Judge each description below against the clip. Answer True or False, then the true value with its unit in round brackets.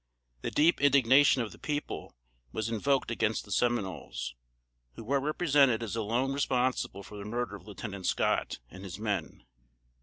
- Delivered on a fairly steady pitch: False (4.8 semitones)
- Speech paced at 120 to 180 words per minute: True (155 wpm)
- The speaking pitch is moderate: False (115 Hz)